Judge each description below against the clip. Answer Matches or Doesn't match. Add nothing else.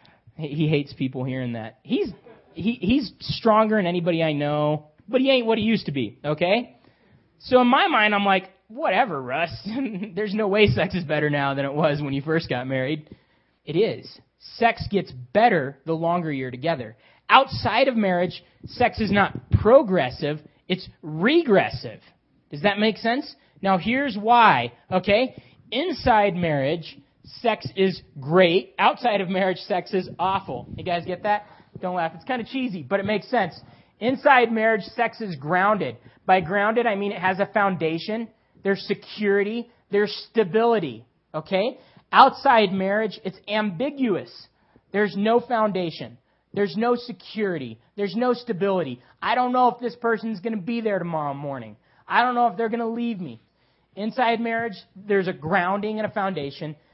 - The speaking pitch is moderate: Doesn't match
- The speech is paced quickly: Doesn't match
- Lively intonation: Matches